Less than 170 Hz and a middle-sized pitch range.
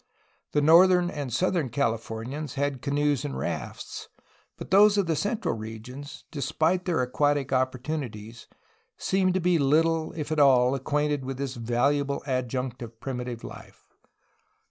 Yes: medium, 140 Hz; average, 4.1 semitones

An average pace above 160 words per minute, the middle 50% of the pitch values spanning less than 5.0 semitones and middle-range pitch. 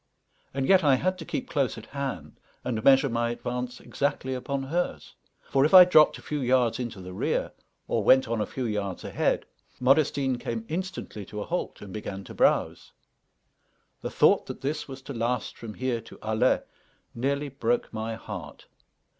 No: average, 180 wpm; average, 3.7 semitones; low, 130 Hz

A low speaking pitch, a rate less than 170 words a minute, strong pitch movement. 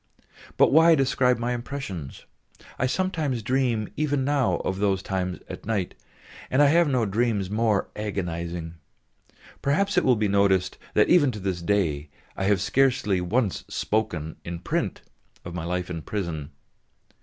Yes: low, 105 Hz; average, 155 wpm; wide, 6.3 semitones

